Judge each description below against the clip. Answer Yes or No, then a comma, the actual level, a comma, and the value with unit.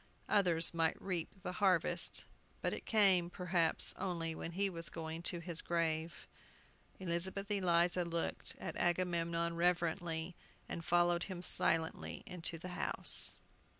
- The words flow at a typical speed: No, slow, 130 wpm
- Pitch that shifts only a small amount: Yes, narrow, 1.4 semitones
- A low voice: No, medium, 170 Hz